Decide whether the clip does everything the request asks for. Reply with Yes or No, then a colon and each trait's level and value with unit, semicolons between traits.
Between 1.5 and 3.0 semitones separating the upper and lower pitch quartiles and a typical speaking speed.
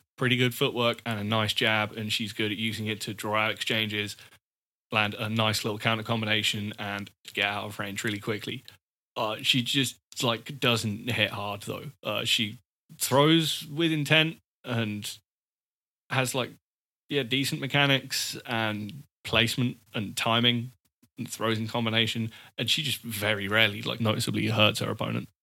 Yes: average, 2.7 semitones; average, 160 wpm